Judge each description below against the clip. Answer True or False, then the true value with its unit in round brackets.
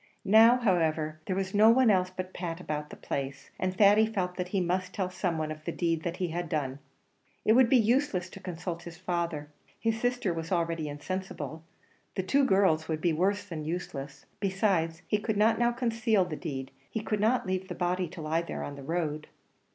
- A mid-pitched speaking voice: True (180 Hz)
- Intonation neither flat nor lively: True (4.2 semitones)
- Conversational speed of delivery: False (210 wpm)